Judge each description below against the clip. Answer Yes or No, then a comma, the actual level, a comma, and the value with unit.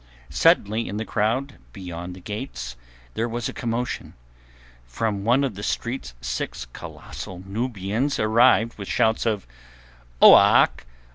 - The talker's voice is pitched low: Yes, low, 110 Hz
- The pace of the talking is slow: Yes, slow, 130 wpm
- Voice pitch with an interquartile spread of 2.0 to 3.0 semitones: No, average, 3.8 semitones